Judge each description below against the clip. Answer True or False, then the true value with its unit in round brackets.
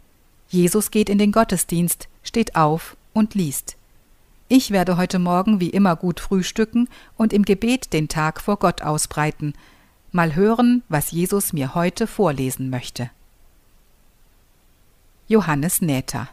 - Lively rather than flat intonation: True (7.7 semitones)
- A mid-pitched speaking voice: True (175 Hz)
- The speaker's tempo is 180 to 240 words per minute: False (130 wpm)